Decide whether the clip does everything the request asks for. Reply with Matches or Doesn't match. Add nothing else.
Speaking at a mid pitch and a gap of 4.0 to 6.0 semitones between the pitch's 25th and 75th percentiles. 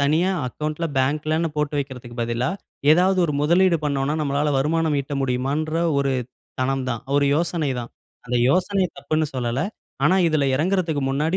Doesn't match